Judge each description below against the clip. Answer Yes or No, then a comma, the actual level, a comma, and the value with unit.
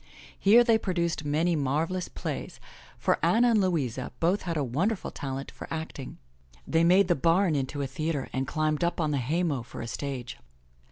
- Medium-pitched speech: Yes, medium, 160 Hz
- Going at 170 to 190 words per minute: Yes, average, 180 wpm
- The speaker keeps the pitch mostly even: No, average, 4.5 semitones